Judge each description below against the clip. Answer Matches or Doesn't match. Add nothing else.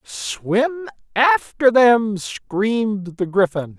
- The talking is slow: Matches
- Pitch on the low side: Doesn't match